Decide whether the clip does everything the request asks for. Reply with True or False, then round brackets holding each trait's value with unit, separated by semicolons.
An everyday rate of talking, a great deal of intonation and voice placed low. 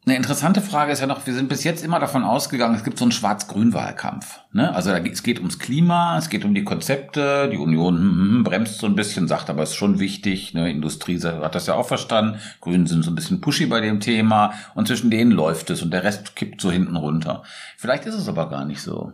False (245 wpm; 8.1 semitones; 115 Hz)